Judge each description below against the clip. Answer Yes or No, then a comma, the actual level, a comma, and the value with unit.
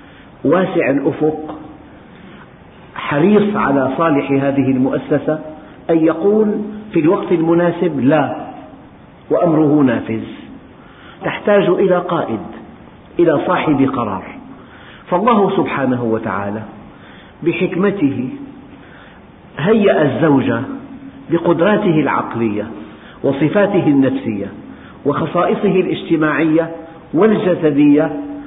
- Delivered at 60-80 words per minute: Yes, average, 70 wpm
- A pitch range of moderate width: Yes, average, 5.0 semitones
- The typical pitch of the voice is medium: Yes, medium, 165 Hz